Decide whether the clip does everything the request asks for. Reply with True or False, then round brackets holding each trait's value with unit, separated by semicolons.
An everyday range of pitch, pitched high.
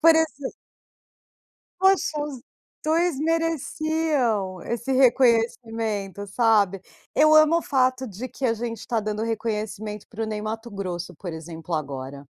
False (6.0 semitones; 230 Hz)